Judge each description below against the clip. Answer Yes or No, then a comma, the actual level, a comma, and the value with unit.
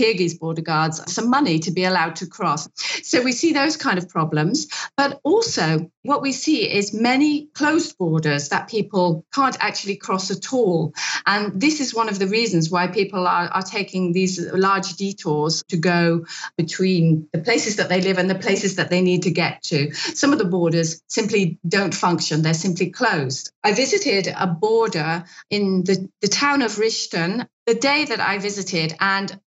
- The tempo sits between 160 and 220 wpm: Yes, average, 185 wpm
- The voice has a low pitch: No, high, 190 Hz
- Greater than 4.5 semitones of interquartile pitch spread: Yes, average, 4.9 semitones